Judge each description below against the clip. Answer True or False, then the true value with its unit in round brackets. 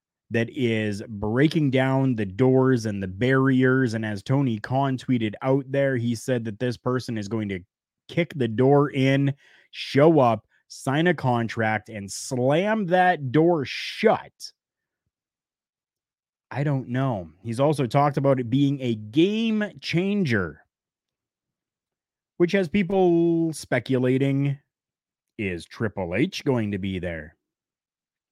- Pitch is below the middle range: True (130 Hz)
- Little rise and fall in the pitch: False (4.0 semitones)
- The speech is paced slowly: True (130 wpm)